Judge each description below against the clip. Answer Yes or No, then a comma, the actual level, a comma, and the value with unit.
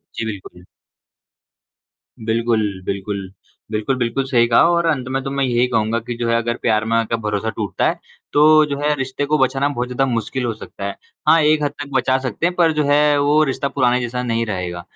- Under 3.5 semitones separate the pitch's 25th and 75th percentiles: No, average, 3.9 semitones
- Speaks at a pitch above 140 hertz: No, low, 125 Hz